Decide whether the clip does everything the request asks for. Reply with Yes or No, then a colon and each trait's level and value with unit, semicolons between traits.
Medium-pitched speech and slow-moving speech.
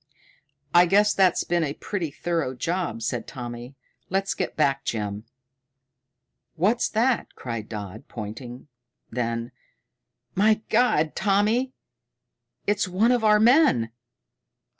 Yes: medium, 170 Hz; slow, 115 wpm